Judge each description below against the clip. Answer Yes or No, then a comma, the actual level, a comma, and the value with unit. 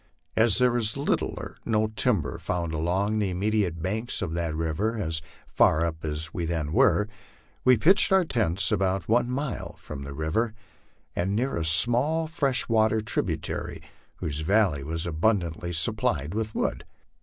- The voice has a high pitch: No, low, 100 Hz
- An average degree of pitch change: No, wide, 5.7 semitones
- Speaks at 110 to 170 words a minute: Yes, average, 160 wpm